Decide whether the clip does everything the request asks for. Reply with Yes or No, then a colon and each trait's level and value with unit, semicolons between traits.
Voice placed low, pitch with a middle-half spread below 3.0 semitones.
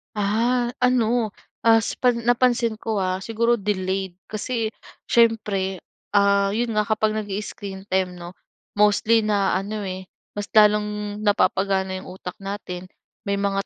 No: high, 210 Hz; narrow, 2.6 semitones